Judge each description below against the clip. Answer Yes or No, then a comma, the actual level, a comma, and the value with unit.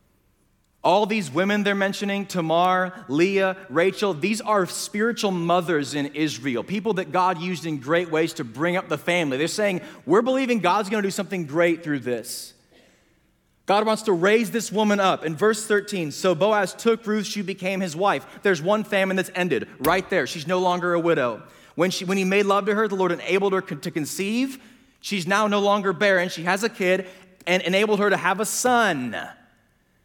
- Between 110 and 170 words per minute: No, average, 195 wpm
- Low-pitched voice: No, high, 190 Hz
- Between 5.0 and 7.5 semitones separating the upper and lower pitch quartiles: No, average, 2.9 semitones